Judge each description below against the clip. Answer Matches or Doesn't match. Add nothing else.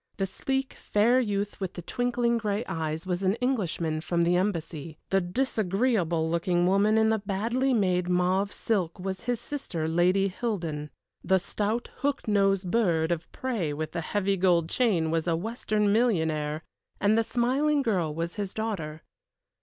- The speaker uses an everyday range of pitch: Matches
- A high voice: Matches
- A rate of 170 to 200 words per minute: Doesn't match